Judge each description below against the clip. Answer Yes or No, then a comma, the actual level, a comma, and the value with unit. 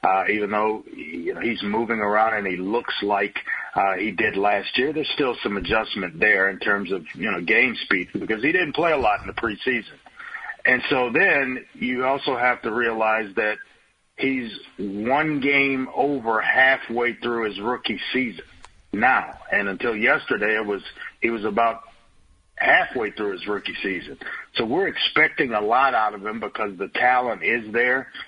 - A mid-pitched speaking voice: No, low, 110 Hz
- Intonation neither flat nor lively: Yes, average, 3.1 semitones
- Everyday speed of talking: Yes, average, 175 wpm